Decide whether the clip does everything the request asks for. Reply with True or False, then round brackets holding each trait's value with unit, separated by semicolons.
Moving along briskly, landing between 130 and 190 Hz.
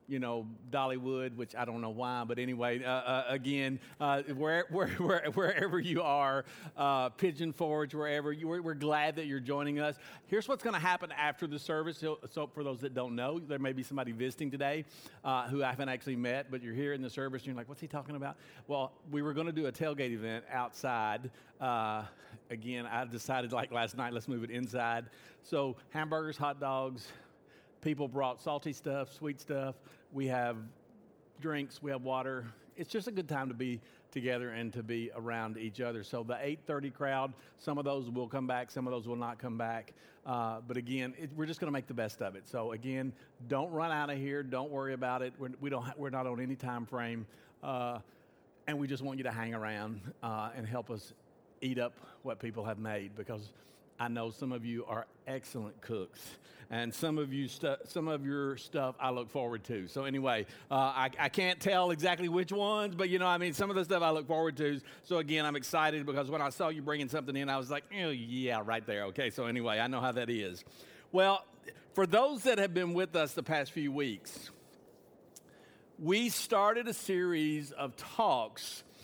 True (215 wpm; 135 Hz)